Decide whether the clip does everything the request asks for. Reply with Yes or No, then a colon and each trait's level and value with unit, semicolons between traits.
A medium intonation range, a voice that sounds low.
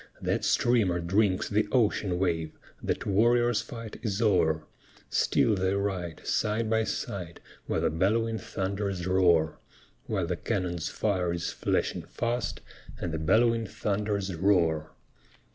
Yes: average, 3.9 semitones; very low, 95 Hz